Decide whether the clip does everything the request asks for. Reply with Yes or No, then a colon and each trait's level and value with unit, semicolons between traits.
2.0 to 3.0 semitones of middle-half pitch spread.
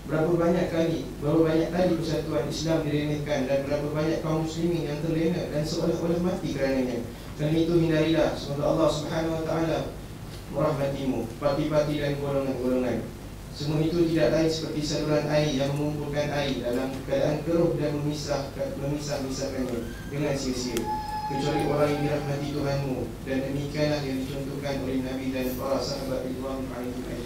Yes: average, 2.7 semitones